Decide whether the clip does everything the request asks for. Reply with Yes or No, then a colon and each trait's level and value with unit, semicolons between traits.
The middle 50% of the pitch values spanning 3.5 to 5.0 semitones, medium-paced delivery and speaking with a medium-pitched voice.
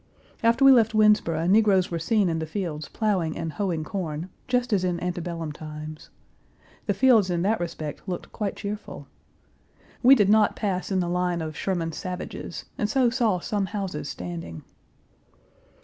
Yes: average, 4.4 semitones; average, 165 wpm; medium, 180 Hz